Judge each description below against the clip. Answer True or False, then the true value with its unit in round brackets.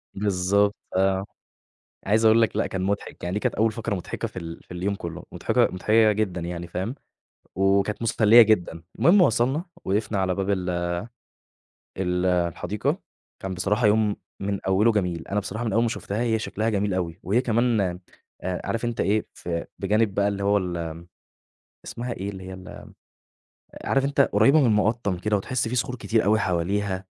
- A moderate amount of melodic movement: True (3.2 semitones)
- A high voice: False (100 Hz)